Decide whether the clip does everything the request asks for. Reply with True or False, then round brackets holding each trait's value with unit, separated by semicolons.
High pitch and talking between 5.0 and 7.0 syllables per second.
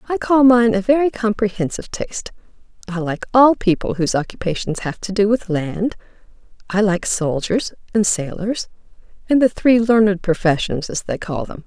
True (205 Hz; 5.2 syllables/s)